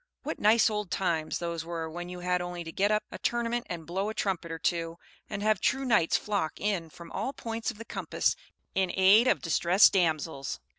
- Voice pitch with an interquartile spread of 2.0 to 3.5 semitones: No, average, 4.0 semitones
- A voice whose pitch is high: No, medium, 180 Hz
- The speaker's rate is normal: No, fast, 210 wpm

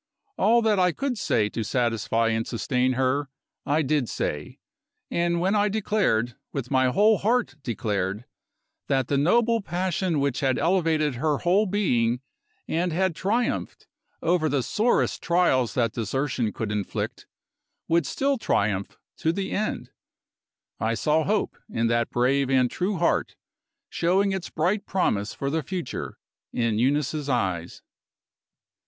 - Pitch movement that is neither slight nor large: No, wide, 7.6 semitones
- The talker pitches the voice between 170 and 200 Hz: No, medium, 145 Hz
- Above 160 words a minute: No, average, 140 wpm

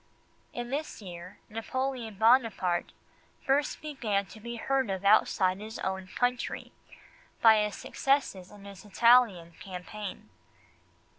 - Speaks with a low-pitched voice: No, high, 215 Hz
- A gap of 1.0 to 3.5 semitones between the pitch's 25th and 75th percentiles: No, average, 4.3 semitones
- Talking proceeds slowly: Yes, slow, 120 wpm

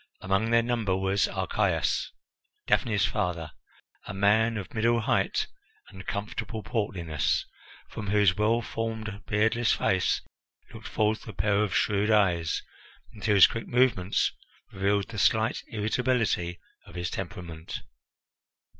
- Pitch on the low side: Yes, low, 105 Hz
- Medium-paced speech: No, slow, 125 wpm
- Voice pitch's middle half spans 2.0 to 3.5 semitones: Yes, average, 2.8 semitones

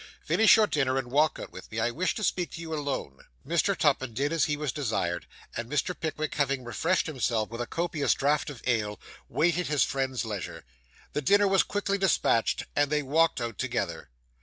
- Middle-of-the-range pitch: Yes, medium, 145 Hz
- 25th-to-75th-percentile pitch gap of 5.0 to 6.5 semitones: Yes, average, 5.3 semitones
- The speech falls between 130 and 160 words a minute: No, average, 200 wpm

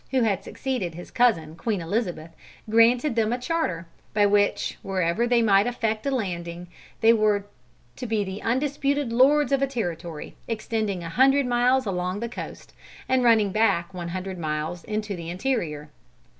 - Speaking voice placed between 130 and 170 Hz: No, high, 215 Hz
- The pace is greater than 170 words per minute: No, average, 165 wpm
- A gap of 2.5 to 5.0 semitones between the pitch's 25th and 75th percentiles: No, wide, 5.5 semitones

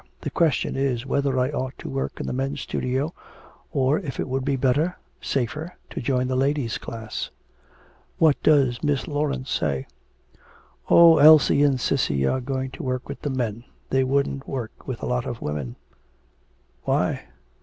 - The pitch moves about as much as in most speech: No, narrow, 2.3 semitones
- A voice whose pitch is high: No, low, 135 Hz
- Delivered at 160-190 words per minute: Yes, average, 165 wpm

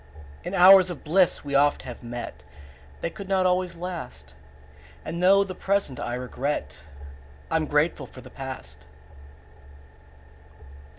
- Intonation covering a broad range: Yes, wide, 6.5 semitones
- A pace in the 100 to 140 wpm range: Yes, slow, 135 wpm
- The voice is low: No, medium, 160 Hz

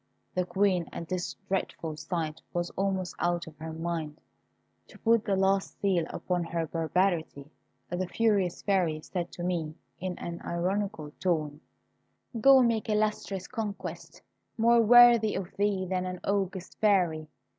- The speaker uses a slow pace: No, average, 145 wpm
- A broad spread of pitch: No, average, 3.1 semitones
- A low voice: No, medium, 185 Hz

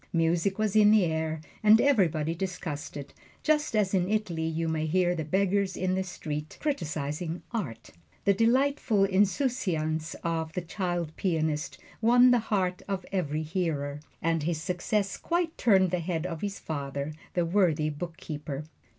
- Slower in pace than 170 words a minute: Yes, average, 155 wpm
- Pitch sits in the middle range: Yes, medium, 175 Hz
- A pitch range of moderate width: Yes, average, 4.0 semitones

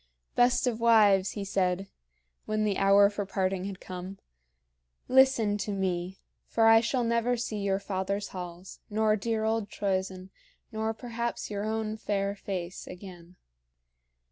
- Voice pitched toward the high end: Yes, high, 200 Hz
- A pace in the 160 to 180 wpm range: No, average, 145 wpm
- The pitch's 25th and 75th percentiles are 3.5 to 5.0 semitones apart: No, narrow, 2.6 semitones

